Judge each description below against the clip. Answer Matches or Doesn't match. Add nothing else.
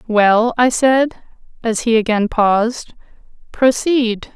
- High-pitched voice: Matches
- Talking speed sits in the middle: Doesn't match